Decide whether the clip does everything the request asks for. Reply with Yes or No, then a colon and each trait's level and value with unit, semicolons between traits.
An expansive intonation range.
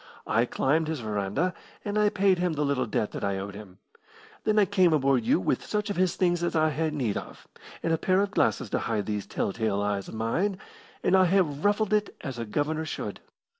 Yes: wide, 8.7 semitones